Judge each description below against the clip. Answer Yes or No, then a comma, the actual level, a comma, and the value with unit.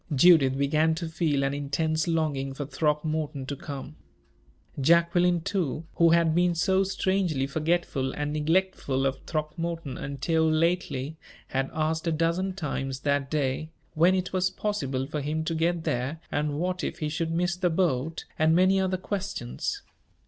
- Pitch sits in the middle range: Yes, medium, 160 Hz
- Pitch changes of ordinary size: Yes, average, 3.5 semitones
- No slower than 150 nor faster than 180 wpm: Yes, average, 155 wpm